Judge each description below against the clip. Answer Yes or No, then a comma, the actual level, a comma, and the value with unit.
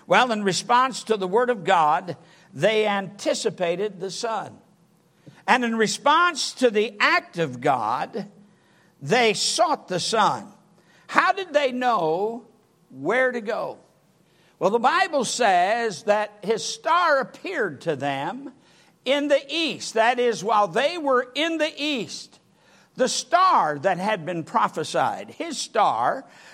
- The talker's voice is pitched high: Yes, high, 225 Hz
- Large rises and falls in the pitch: Yes, wide, 6.1 semitones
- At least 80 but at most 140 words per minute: Yes, slow, 135 wpm